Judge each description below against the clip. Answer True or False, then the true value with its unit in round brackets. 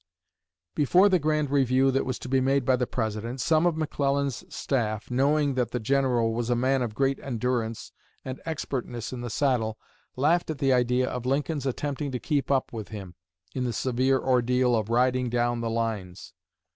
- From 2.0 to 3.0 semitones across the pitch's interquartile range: True (2.6 semitones)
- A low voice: True (130 Hz)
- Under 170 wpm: False (185 wpm)